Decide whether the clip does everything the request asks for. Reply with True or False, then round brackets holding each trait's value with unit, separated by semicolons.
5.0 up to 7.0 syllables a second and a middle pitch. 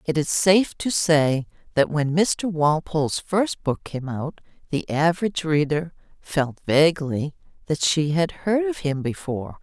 False (4.3 syllables/s; 160 Hz)